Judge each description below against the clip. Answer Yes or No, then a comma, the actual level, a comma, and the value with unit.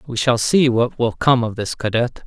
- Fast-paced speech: Yes, fast, 240 wpm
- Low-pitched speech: Yes, low, 120 Hz